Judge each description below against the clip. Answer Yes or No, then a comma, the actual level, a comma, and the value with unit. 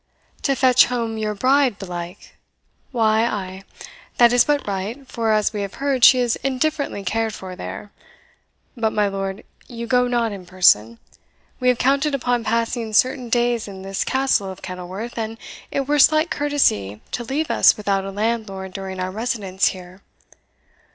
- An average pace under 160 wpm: No, average, 165 wpm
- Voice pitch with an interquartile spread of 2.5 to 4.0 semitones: No, average, 4.4 semitones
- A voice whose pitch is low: No, high, 225 Hz